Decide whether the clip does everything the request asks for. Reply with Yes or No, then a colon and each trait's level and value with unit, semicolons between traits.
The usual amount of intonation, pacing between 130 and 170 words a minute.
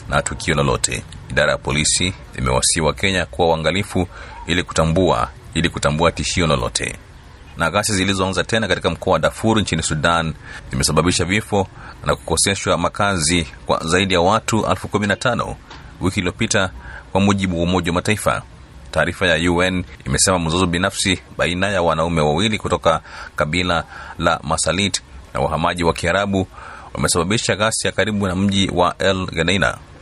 Yes: average, 3.5 semitones; fast, 140 wpm